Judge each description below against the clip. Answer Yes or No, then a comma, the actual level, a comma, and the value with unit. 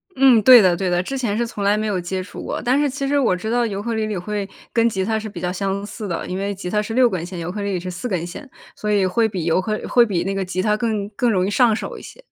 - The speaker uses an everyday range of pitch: Yes, average, 3.7 semitones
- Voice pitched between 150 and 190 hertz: No, high, 205 Hz